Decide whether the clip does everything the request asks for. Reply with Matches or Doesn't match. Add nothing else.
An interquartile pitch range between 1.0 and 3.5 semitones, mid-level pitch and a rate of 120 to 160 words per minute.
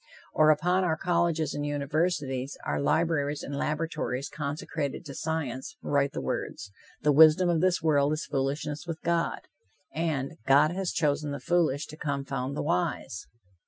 Matches